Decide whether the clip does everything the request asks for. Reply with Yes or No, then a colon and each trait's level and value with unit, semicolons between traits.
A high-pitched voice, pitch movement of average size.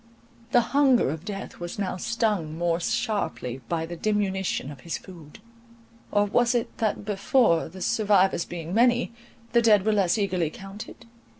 Yes: high, 195 Hz; average, 4.6 semitones